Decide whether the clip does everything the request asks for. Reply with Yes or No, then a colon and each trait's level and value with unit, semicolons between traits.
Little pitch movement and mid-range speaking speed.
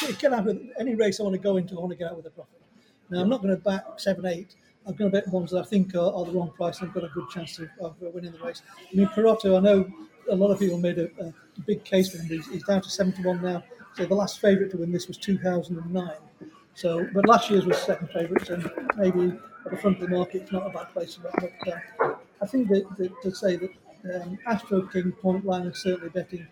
No: narrow, 2.1 semitones; fast, 275 wpm